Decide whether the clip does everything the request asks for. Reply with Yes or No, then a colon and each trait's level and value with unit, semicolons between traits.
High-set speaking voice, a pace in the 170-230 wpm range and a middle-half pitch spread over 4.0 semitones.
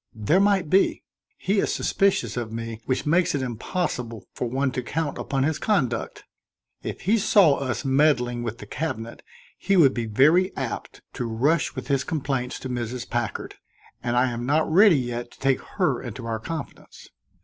No: low, 130 Hz; average, 180 wpm; average, 4.9 semitones